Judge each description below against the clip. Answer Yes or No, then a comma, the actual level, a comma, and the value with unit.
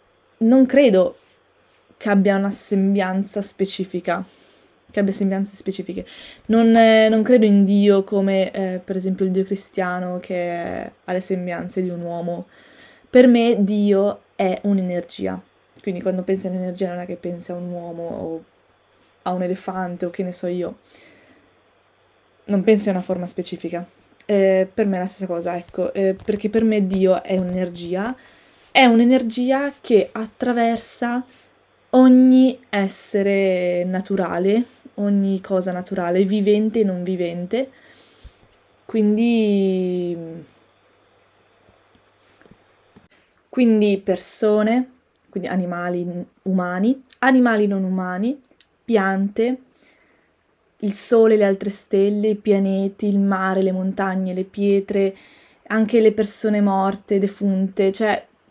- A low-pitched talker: No, high, 195 Hz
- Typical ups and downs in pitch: Yes, average, 3.0 semitones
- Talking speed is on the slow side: No, average, 125 wpm